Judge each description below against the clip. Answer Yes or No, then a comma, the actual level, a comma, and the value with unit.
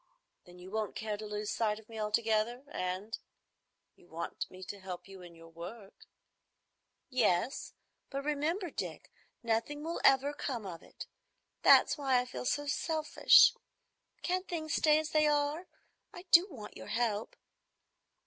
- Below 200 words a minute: Yes, average, 150 wpm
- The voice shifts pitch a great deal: Yes, wide, 6.4 semitones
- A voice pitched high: Yes, high, 230 Hz